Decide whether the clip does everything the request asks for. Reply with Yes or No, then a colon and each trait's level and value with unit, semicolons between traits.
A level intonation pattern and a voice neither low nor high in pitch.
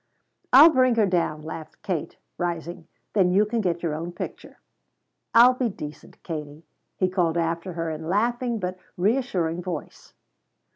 No: average, 4.7 semitones; medium, 180 Hz